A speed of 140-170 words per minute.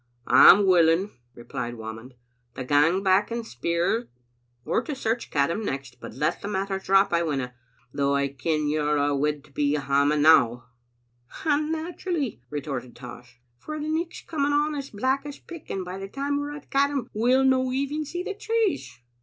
No: average, 180 wpm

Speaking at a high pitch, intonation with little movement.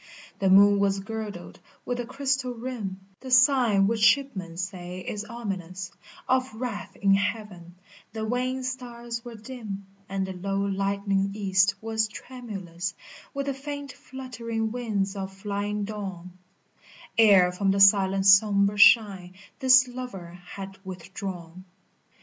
No: high, 205 Hz; average, 3.7 semitones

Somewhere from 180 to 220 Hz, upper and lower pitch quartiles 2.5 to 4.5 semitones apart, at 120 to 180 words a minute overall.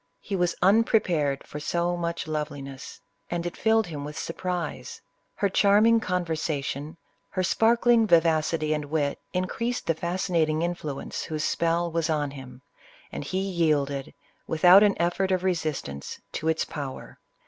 No: medium, 170 Hz; average, 3.5 semitones; average, 150 wpm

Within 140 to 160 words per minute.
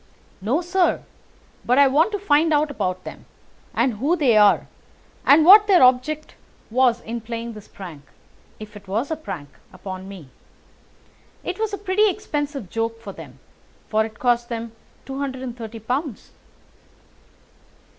Yes: average, 145 wpm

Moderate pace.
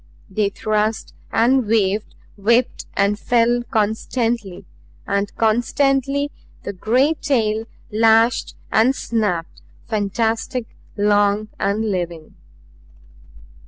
No: slow, 90 wpm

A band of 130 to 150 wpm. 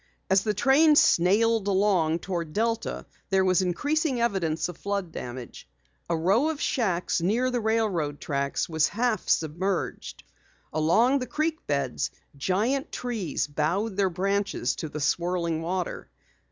Yes: average, 140 wpm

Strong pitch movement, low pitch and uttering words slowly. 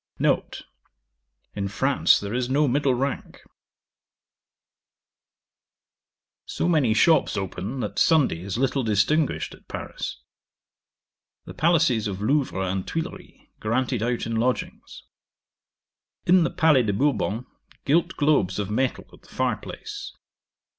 Yes: wide, 6.2 semitones; low, 125 Hz; slow, 120 wpm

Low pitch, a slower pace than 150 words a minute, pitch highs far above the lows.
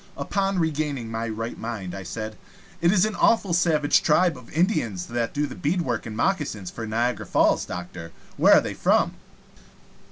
No: low, 120 Hz; average, 170 wpm; wide, 7.5 semitones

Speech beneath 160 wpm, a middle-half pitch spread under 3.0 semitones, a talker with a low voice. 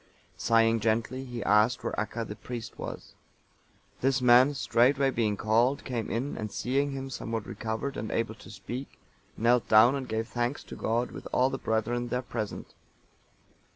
No: average, 165 wpm; narrow, 2.6 semitones; low, 120 Hz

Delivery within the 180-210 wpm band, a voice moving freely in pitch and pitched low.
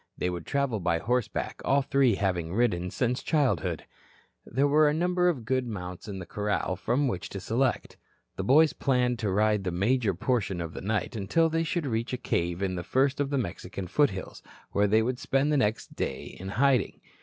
Yes: average, 200 wpm; wide, 6.2 semitones; low, 115 Hz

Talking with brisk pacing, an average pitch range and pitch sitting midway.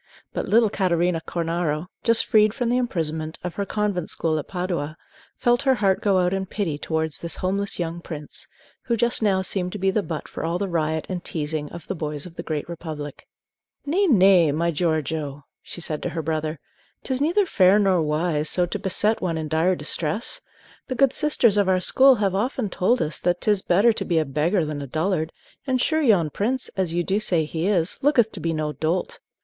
Yes: fast, 215 wpm; average, 4.6 semitones; medium, 180 Hz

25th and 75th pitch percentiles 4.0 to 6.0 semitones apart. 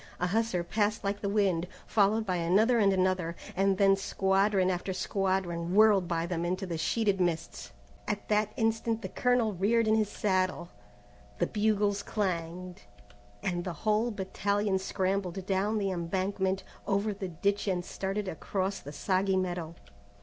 No: narrow, 2.4 semitones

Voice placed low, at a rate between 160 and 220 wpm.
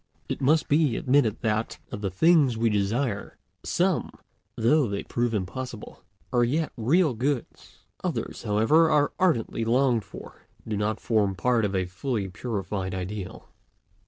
No: low, 115 Hz; average, 145 wpm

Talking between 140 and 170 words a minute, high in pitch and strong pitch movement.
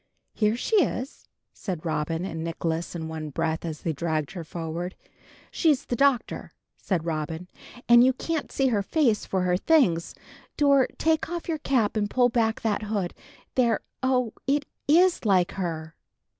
Yes: average, 165 wpm; high, 205 Hz; wide, 7.8 semitones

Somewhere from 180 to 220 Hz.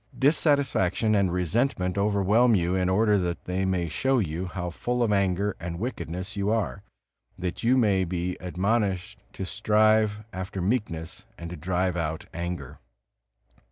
No: very low, 95 Hz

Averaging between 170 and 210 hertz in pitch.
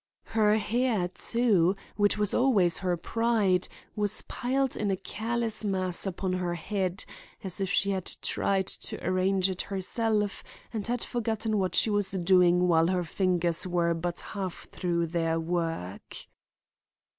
Yes: high, 190 Hz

